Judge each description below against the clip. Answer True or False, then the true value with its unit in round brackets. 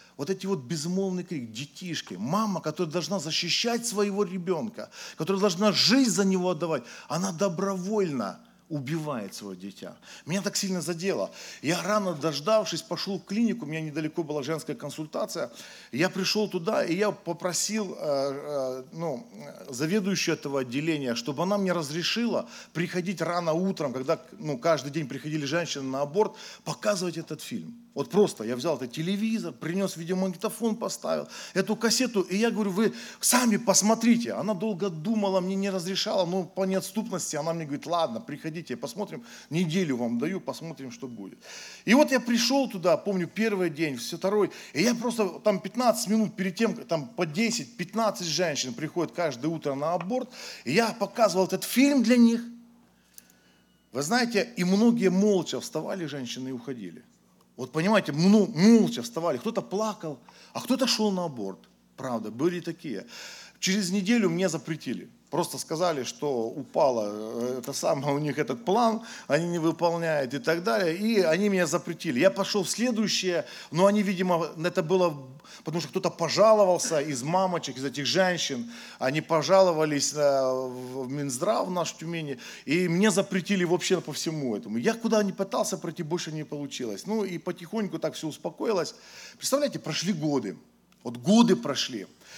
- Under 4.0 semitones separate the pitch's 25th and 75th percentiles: False (4.9 semitones)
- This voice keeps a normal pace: True (155 wpm)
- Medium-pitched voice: True (180 Hz)